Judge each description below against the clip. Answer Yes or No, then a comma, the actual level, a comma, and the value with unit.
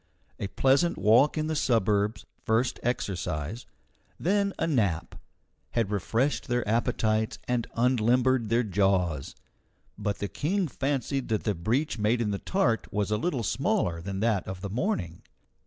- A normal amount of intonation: Yes, average, 4.4 semitones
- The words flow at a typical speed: Yes, average, 150 wpm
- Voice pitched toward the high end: No, low, 115 Hz